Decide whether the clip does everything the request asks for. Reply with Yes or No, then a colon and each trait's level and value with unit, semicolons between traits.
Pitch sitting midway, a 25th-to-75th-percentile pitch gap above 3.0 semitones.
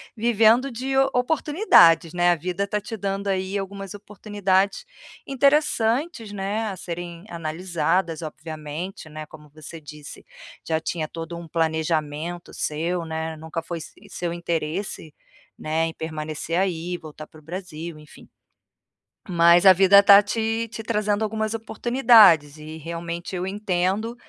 Yes: medium, 175 Hz; average, 4.4 semitones